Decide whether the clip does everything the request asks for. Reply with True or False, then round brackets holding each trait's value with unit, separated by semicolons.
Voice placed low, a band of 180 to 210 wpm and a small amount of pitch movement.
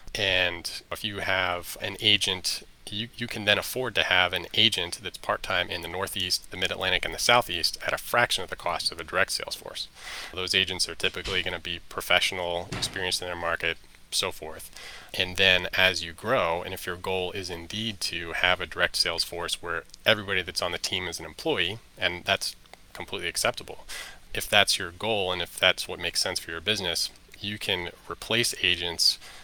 True (90 Hz; 200 wpm; 2.0 semitones)